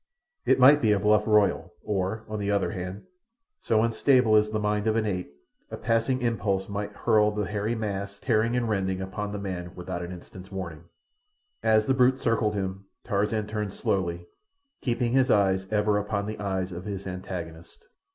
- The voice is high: No, low, 105 Hz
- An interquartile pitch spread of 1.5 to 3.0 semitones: Yes, narrow, 2.5 semitones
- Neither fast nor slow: Yes, average, 180 wpm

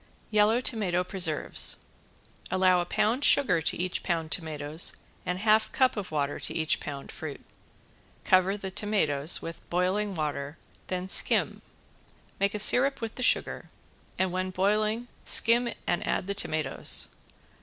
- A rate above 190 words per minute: No, average, 145 wpm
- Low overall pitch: No, medium, 185 Hz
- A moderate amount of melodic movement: Yes, average, 4.6 semitones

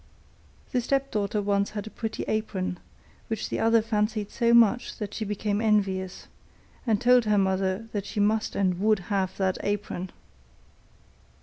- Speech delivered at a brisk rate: No, average, 150 wpm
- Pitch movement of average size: No, narrow, 2.2 semitones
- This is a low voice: No, high, 210 Hz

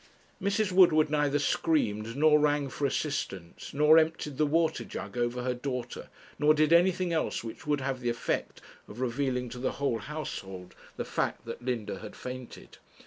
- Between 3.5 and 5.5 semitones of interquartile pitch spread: Yes, average, 4.2 semitones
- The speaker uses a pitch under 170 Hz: Yes, medium, 140 Hz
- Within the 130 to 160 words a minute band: No, average, 170 wpm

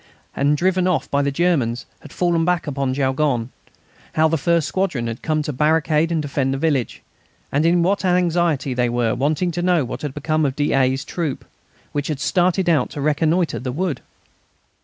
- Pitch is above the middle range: No, medium, 150 Hz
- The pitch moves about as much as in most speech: Yes, average, 4.1 semitones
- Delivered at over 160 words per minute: Yes, average, 185 wpm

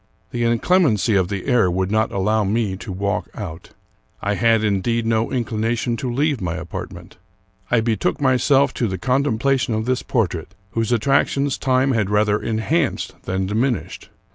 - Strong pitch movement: No, average, 4.0 semitones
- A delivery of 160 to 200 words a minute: Yes, average, 165 wpm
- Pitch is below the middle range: Yes, low, 115 Hz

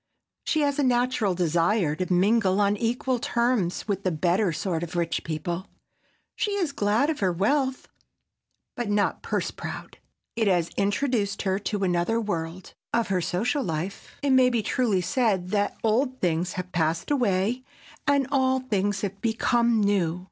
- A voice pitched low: No, high, 205 Hz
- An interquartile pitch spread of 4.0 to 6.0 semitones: Yes, average, 5.1 semitones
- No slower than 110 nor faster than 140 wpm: No, average, 160 wpm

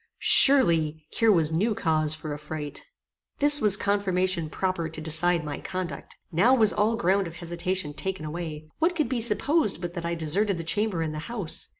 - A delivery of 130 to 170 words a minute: No, average, 185 wpm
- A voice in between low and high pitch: Yes, medium, 175 Hz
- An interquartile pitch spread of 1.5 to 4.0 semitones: No, average, 4.6 semitones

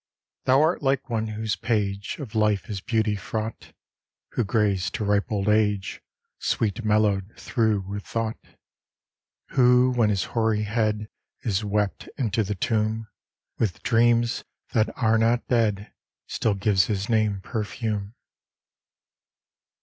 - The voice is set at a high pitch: No, low, 110 Hz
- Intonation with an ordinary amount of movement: No, narrow, 1.9 semitones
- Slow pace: Yes, slow, 130 wpm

